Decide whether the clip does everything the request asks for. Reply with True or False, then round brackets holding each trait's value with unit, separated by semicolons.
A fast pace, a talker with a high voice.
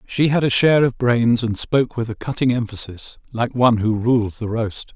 False (220 wpm; 120 Hz)